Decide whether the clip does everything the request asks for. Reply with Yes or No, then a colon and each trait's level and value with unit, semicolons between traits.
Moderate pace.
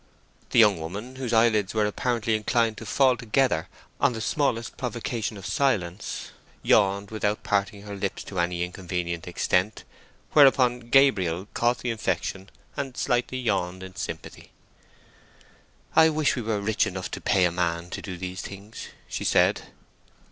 Yes: average, 155 wpm